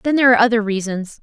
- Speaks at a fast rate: Yes, fast, 245 wpm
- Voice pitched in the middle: No, high, 220 Hz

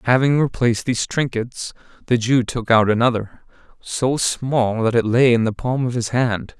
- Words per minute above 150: Yes, average, 180 wpm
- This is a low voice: Yes, low, 120 Hz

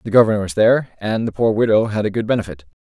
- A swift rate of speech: Yes, fast, 255 wpm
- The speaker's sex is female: No, male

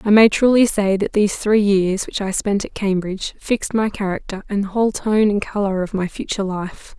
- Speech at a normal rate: No, fast, 225 wpm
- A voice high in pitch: Yes, high, 200 Hz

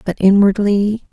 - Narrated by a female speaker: Yes, female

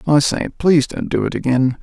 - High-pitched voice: No, medium, 140 Hz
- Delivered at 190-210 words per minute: No, fast, 230 wpm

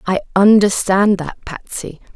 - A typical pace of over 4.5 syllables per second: No, 4.1 syllables/s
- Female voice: Yes, female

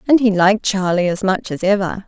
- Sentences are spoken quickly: Yes, fast, 230 wpm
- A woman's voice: Yes, female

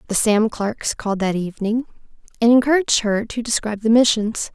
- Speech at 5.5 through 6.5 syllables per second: Yes, 5.8 syllables/s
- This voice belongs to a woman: Yes, female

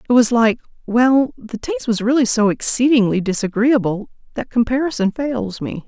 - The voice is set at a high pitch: Yes, high, 235 Hz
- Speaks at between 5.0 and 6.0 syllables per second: Yes, 5.1 syllables/s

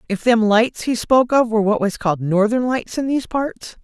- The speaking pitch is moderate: No, high, 230 Hz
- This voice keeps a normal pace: No, fast, 235 wpm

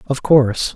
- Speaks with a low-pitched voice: Yes, low, 130 Hz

